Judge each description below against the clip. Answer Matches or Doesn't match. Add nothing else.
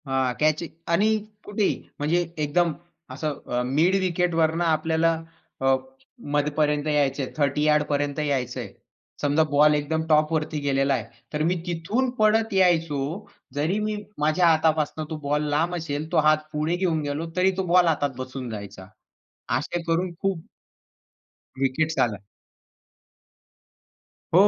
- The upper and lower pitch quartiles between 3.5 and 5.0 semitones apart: Doesn't match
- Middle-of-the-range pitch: Matches